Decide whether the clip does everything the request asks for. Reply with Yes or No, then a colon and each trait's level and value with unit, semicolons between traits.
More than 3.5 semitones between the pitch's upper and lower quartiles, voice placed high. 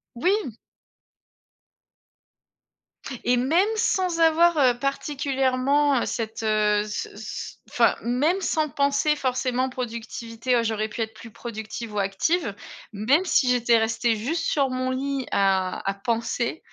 Yes: average, 4.2 semitones; very high, 250 Hz